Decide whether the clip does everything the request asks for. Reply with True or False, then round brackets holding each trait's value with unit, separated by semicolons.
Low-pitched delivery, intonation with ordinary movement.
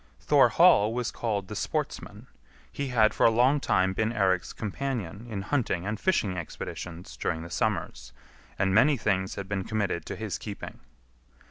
True (105 Hz; 3.4 semitones)